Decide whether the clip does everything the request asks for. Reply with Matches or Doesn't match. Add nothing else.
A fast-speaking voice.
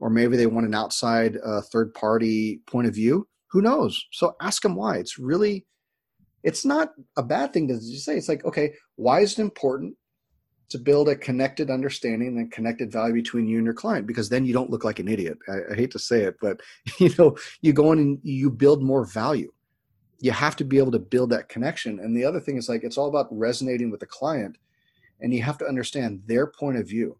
Matches